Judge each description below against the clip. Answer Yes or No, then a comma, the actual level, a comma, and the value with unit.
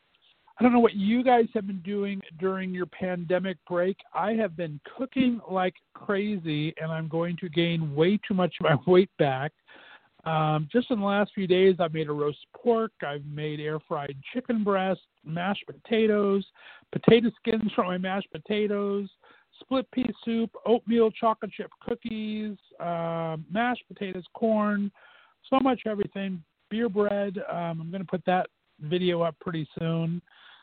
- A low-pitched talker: No, high, 195 Hz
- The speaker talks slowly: No, average, 165 wpm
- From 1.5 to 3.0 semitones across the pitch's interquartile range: No, average, 4.4 semitones